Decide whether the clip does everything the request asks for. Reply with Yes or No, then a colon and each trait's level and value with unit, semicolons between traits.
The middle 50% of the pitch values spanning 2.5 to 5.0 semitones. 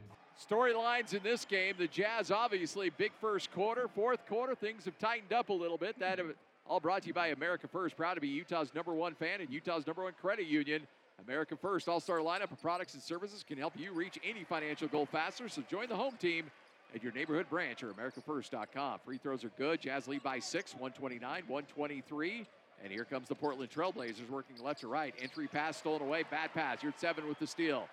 No: wide, 5.5 semitones